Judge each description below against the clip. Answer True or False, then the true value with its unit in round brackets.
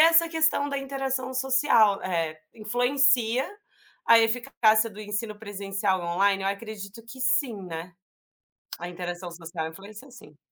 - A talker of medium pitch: False (215 Hz)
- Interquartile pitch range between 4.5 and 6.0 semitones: True (5.3 semitones)